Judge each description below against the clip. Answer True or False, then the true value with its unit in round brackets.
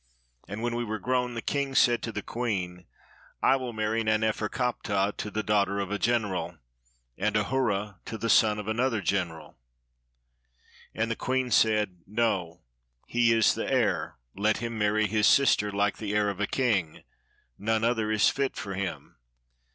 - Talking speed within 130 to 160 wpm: False (175 wpm)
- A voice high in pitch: False (110 Hz)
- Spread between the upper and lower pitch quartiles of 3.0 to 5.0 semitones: False (2.5 semitones)